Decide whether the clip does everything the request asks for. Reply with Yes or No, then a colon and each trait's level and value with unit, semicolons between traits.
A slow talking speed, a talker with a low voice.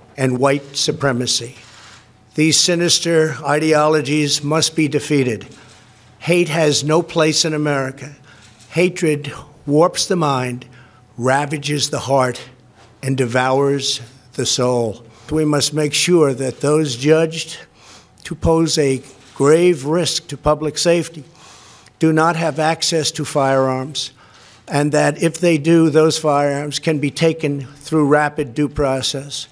No: slow, 125 wpm; medium, 145 Hz